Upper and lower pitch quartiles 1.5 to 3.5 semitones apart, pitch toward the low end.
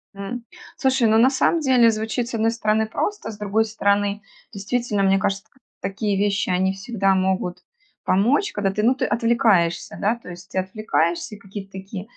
No: average, 2.9 semitones; high, 205 Hz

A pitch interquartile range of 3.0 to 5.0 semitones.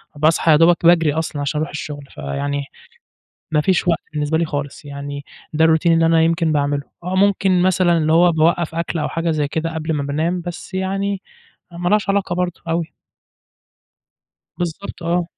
No: narrow, 2.6 semitones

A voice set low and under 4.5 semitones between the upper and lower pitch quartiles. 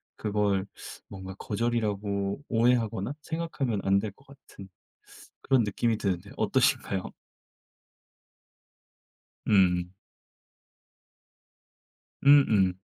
Yes: low, 105 Hz; average, 3.5 semitones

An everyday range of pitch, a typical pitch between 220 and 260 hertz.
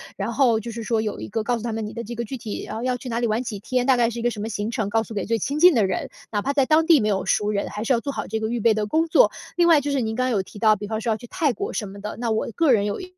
Yes: average, 3.1 semitones; high, 230 Hz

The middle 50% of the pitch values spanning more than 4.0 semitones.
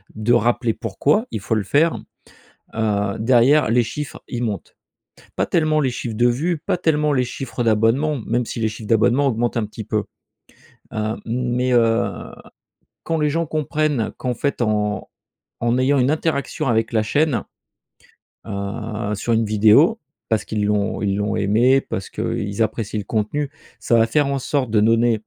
Yes: average, 4.5 semitones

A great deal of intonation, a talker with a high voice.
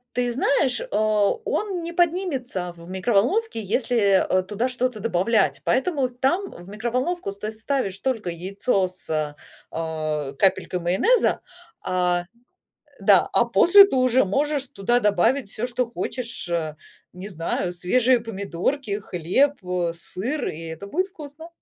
Yes: wide, 6.5 semitones; high, 220 Hz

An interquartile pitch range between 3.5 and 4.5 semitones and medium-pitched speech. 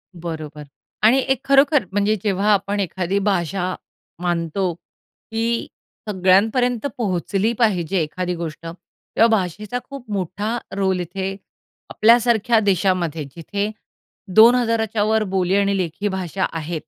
No: average, 3.8 semitones; high, 195 Hz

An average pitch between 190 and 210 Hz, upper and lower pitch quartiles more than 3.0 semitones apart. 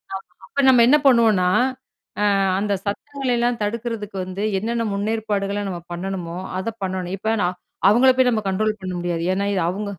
Yes: high, 205 Hz; average, 3.6 semitones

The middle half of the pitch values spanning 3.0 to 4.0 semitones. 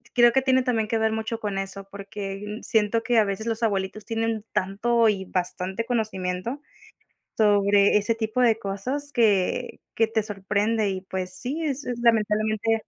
No: narrow, 2.6 semitones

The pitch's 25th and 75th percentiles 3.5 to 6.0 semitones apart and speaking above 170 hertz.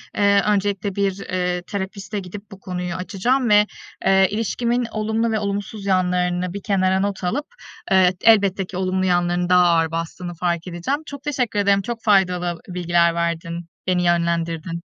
No: narrow, 2.5 semitones; high, 190 Hz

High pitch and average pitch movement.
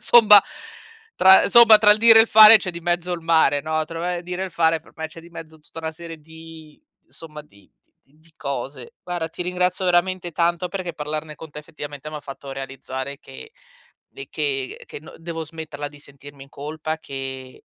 No: medium, 160 Hz; average, 3.4 semitones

